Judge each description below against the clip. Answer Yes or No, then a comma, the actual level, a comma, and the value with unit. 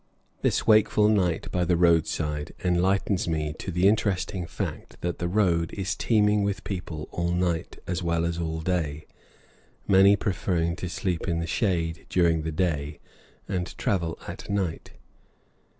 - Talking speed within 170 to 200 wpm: No, average, 150 wpm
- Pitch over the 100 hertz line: No, very low, 90 Hz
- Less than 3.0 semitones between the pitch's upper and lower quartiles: Yes, narrow, 2.6 semitones